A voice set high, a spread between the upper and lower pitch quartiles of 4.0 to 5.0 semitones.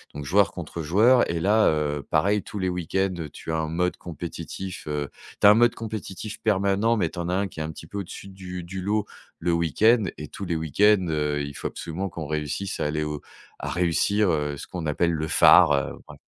No: very low, 90 Hz; average, 4.3 semitones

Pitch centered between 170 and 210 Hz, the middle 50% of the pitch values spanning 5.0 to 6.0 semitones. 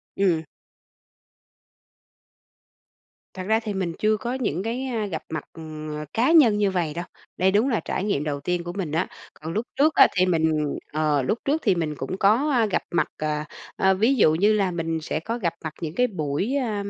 Yes: medium, 185 Hz; wide, 5.6 semitones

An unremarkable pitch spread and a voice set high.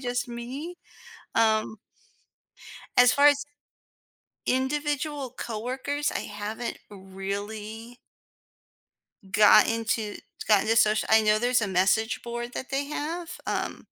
Yes: average, 3.9 semitones; high, 235 Hz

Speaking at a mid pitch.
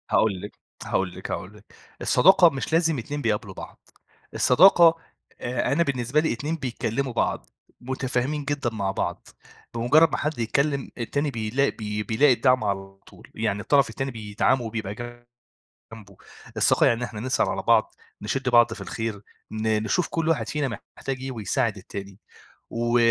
No: low, 120 Hz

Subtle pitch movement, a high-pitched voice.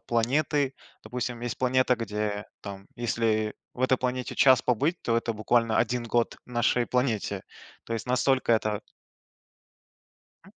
No: narrow, 2.3 semitones; low, 120 Hz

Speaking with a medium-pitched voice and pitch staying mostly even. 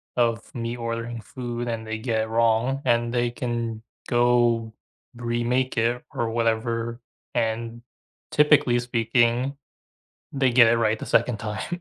No: low, 120 Hz; narrow, 1.0 semitones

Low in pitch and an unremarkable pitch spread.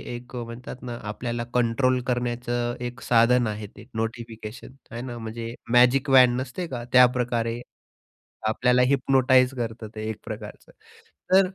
No: low, 120 Hz; narrow, 1.5 semitones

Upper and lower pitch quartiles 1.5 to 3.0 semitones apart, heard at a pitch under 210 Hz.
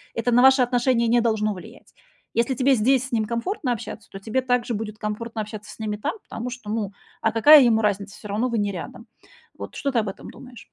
No: average, 2.7 semitones; high, 230 Hz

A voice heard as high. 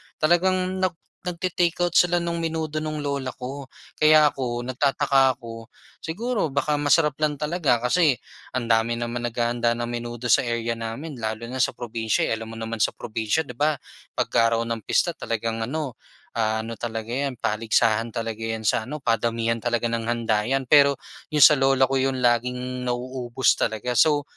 No: low, 125 Hz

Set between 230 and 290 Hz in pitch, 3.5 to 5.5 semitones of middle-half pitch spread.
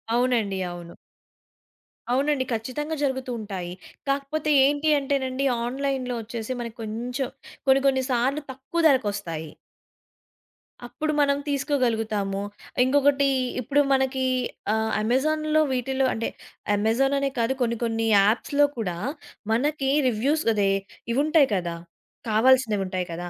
Yes: very high, 255 Hz; average, 4.1 semitones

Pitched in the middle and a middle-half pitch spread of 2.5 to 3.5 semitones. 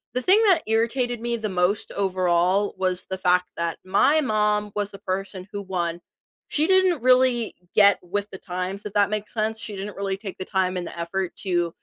No: high, 200 Hz; average, 3.2 semitones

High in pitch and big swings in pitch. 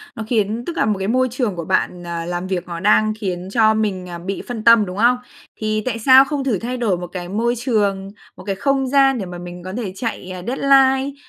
No: high, 215 Hz; average, 5.0 semitones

